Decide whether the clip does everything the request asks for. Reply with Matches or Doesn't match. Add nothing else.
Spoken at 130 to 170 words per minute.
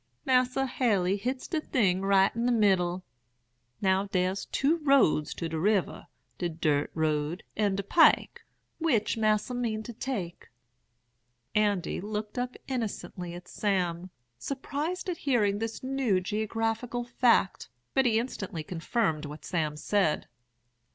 Matches